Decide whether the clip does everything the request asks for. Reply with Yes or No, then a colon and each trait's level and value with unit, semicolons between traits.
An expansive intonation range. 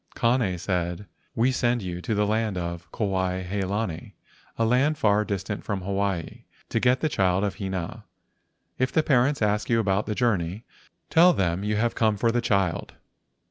No: average, 3.8 semitones